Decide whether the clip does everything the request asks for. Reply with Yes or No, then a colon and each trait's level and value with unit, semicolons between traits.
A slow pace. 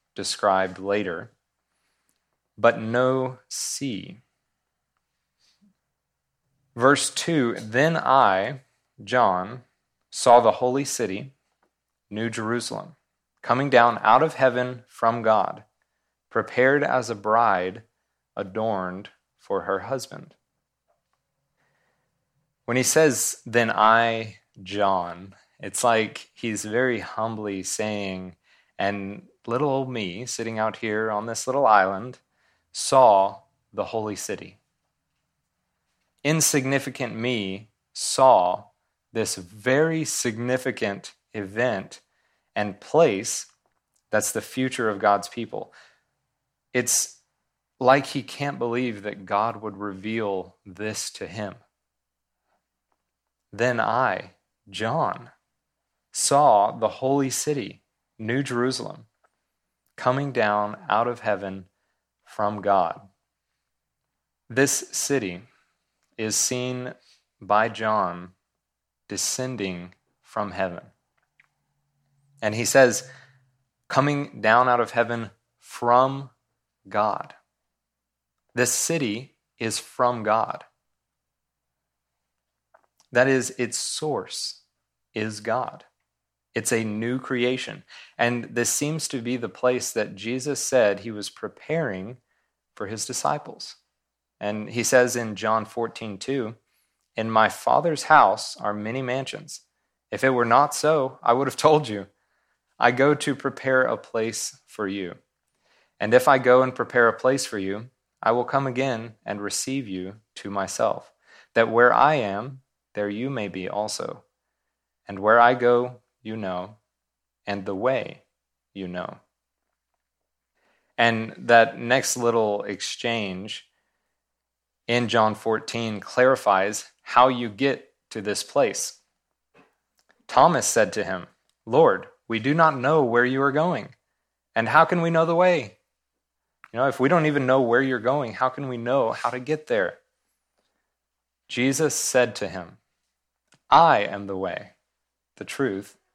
Yes: slow, 115 wpm